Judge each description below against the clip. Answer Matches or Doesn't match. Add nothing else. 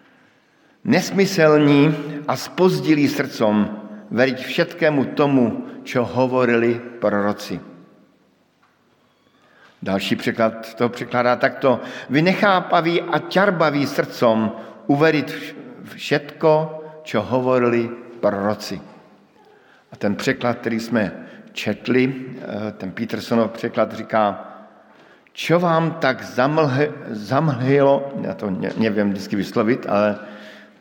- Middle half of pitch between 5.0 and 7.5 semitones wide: Matches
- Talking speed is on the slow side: Matches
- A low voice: Matches